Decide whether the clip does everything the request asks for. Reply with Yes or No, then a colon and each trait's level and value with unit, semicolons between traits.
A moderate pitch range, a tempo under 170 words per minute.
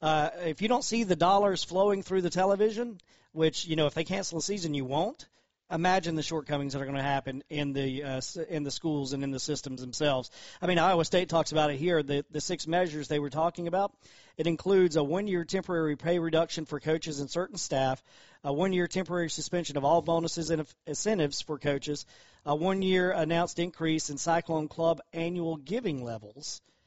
No: average, 3.4 semitones; average, 200 wpm